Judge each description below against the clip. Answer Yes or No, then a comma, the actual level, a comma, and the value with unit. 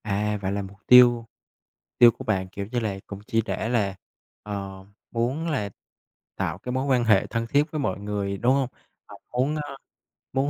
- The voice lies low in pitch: Yes, low, 115 Hz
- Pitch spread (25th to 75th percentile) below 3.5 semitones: No, average, 4.5 semitones